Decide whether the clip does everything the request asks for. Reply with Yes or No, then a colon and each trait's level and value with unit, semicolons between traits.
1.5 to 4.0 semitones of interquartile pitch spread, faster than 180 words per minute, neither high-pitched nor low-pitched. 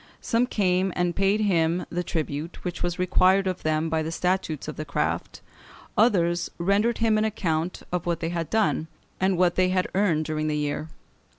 Yes: average, 3.1 semitones; average, 190 wpm; medium, 175 Hz